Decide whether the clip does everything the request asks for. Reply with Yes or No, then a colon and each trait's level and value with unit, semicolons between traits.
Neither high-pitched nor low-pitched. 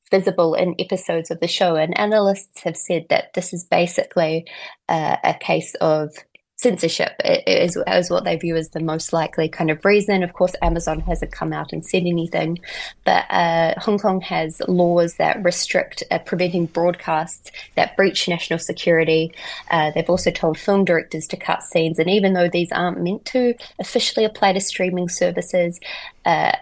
Yes: medium, 175 Hz